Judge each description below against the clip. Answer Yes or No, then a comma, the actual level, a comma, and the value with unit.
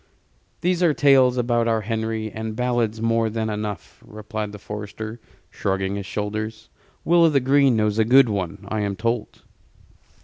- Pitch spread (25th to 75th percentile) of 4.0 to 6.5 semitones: No, narrow, 2.6 semitones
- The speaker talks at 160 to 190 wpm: Yes, average, 165 wpm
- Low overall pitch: Yes, low, 110 Hz